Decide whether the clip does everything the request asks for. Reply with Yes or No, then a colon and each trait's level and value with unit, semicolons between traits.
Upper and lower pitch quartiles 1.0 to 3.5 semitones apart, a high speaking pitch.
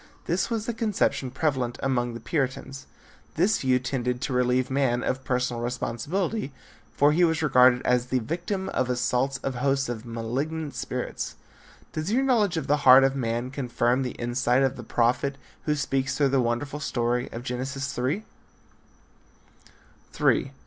No: average, 3.1 semitones; low, 130 Hz